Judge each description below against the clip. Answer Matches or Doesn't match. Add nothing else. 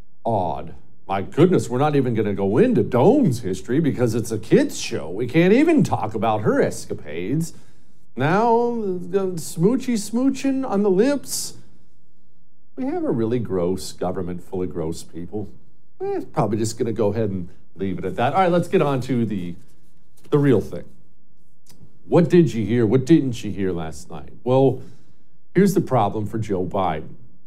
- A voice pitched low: Matches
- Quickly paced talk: Doesn't match